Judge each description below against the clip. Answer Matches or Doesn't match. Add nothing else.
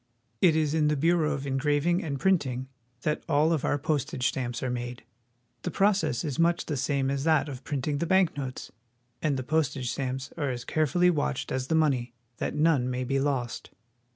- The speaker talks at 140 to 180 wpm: Doesn't match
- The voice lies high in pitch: Doesn't match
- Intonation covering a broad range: Doesn't match